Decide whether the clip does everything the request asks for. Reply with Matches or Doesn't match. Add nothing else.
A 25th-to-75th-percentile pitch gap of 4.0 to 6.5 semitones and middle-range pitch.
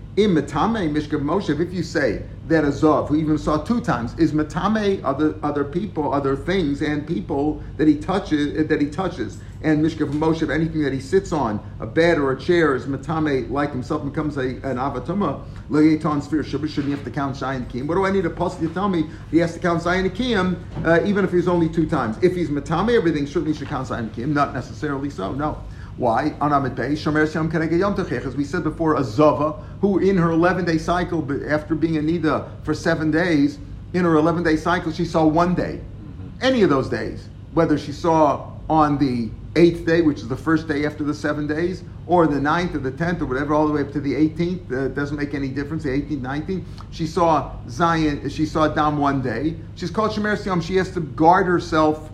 Doesn't match